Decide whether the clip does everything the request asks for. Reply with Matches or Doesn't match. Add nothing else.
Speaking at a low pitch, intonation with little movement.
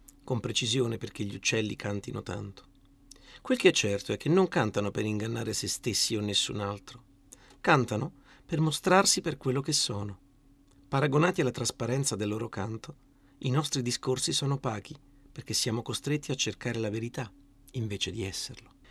Doesn't match